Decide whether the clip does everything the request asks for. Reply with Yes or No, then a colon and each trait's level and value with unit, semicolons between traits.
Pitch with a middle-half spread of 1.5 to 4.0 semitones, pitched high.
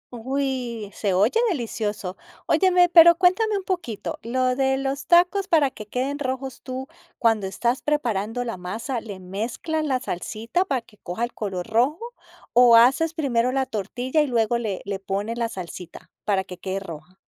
No: average, 5.1 semitones; high, 240 Hz